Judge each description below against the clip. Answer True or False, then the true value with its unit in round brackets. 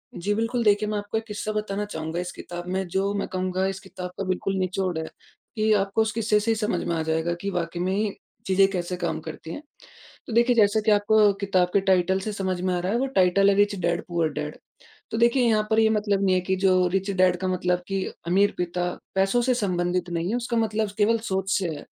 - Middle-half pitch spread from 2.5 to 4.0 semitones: True (2.8 semitones)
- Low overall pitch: False (195 Hz)